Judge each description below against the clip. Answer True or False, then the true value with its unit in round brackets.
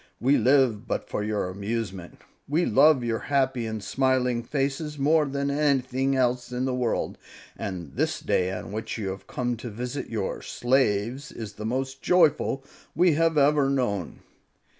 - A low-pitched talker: True (125 Hz)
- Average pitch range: True (4.1 semitones)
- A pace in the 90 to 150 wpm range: False (160 wpm)